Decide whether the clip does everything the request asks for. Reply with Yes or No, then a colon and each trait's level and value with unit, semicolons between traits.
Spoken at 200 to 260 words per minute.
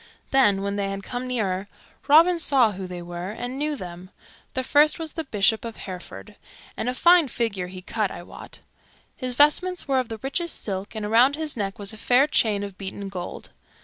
Yes: fast, 205 wpm